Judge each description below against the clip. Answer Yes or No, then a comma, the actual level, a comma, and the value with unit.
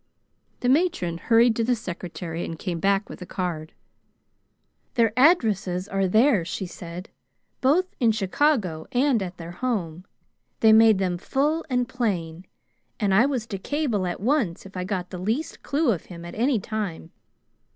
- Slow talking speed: No, average, 165 wpm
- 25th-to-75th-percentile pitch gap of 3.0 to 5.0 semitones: No, wide, 5.6 semitones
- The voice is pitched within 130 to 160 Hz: No, high, 205 Hz